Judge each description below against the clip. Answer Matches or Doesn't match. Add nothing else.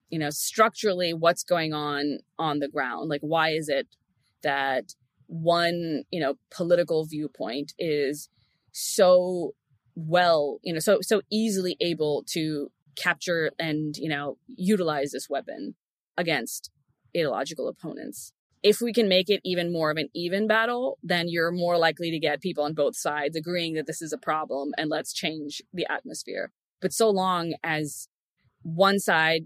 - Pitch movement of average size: Matches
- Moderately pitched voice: Matches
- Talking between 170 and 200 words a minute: Doesn't match